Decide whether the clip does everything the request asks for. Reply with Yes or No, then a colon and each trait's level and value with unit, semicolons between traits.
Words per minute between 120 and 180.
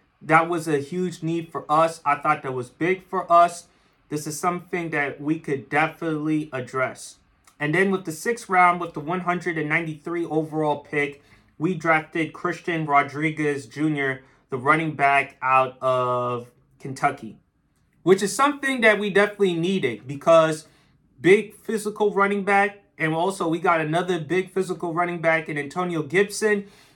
Yes: average, 150 wpm